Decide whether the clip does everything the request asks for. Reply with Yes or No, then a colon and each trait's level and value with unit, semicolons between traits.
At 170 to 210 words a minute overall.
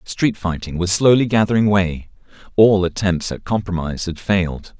No: average, 150 wpm